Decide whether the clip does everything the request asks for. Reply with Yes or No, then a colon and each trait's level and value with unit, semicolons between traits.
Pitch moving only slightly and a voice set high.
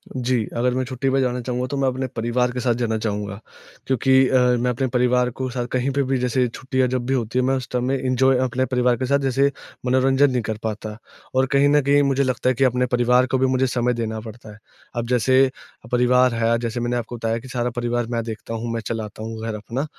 No: narrow, 1.8 semitones; low, 125 Hz